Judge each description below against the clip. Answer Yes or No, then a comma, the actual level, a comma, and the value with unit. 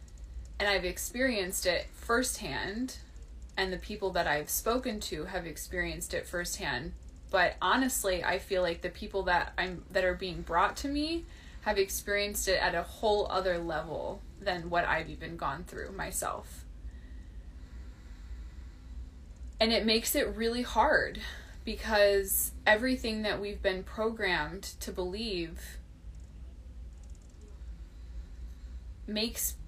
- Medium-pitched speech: Yes, medium, 180 Hz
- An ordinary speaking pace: No, slow, 125 wpm